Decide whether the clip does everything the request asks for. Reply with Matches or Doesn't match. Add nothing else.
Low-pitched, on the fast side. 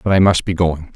Matches